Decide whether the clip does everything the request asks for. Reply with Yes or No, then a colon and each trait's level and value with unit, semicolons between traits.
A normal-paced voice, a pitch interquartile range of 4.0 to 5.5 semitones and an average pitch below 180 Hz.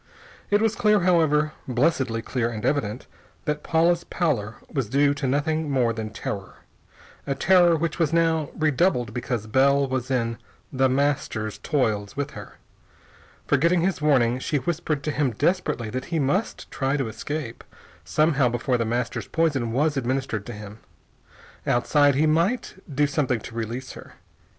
Yes: average, 155 wpm; average, 4.6 semitones; medium, 140 Hz